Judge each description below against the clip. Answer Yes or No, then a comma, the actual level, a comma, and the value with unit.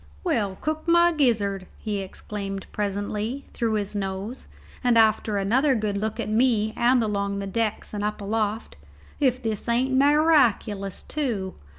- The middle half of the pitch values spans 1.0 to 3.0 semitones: No, average, 3.9 semitones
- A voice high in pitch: Yes, high, 215 Hz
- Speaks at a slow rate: No, average, 155 wpm